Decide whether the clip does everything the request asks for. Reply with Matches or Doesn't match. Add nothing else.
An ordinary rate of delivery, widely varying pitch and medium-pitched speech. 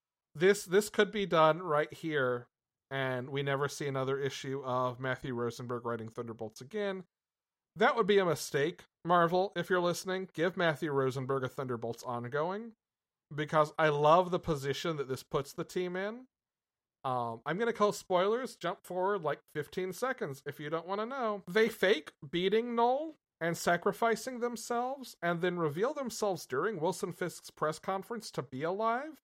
Matches